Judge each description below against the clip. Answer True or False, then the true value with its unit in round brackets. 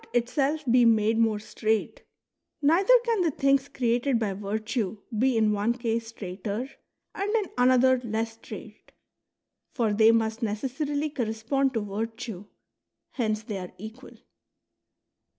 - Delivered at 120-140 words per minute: True (135 wpm)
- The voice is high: True (230 Hz)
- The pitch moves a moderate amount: True (3.5 semitones)